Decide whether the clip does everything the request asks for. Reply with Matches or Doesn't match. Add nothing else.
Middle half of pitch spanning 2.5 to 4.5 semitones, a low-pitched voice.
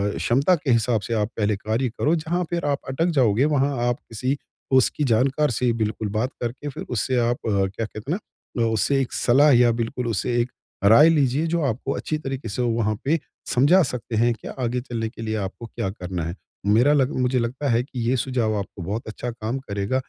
Matches